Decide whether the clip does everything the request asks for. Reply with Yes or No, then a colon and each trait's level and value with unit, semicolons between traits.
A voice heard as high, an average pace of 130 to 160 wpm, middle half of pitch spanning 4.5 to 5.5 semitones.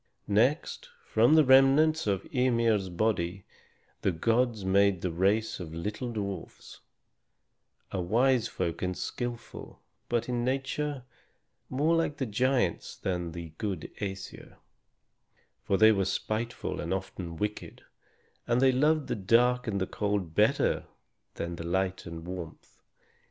No: low, 105 Hz; slow, 135 wpm; average, 5.2 semitones